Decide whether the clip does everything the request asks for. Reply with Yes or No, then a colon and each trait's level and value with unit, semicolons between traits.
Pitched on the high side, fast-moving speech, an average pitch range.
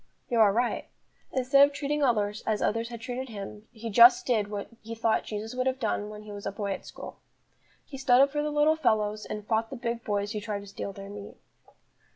Yes: high, 225 Hz; fast, 230 wpm; average, 3.4 semitones